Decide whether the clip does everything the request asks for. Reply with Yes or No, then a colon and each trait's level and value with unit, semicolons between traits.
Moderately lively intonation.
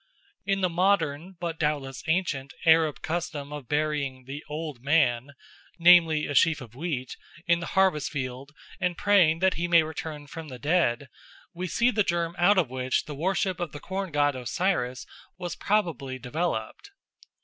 Yes: average, 4.0 semitones